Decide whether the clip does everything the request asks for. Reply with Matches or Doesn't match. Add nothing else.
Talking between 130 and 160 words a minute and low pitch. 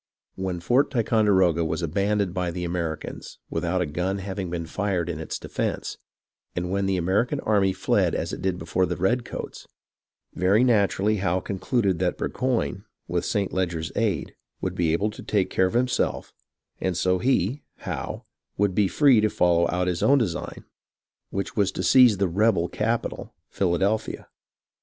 Doesn't match